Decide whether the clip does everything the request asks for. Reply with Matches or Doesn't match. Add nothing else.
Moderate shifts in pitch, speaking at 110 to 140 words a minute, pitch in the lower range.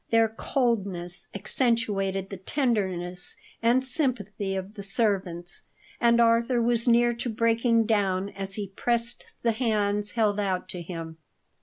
Doesn't match